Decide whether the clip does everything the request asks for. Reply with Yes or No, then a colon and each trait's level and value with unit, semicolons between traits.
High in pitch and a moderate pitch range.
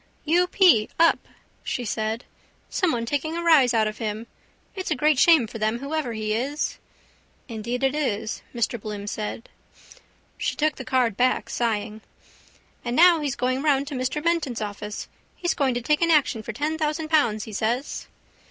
No: very high, 255 Hz; wide, 5.7 semitones